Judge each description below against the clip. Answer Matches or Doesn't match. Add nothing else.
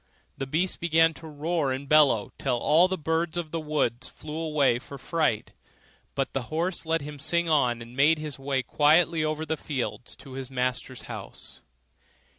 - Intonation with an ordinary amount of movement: Matches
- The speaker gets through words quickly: Doesn't match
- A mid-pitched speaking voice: Matches